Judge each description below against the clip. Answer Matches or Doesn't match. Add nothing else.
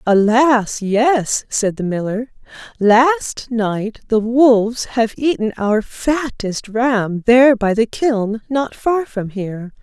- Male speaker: Doesn't match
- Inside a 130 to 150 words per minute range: Matches